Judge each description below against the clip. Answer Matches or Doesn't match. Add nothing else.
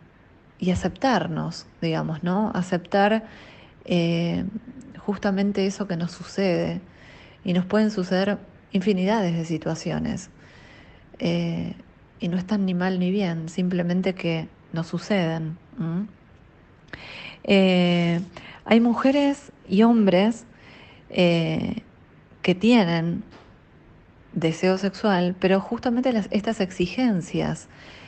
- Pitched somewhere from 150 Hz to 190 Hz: Matches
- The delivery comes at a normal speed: Doesn't match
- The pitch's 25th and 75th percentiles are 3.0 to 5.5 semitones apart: Matches